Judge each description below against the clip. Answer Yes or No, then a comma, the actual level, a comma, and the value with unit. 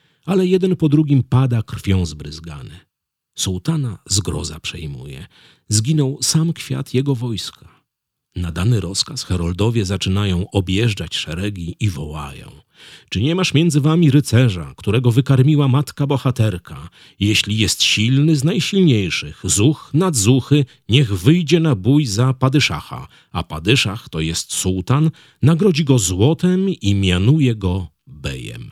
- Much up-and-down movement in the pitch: Yes, wide, 7.5 semitones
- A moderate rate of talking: Yes, average, 125 wpm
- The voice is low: Yes, low, 120 Hz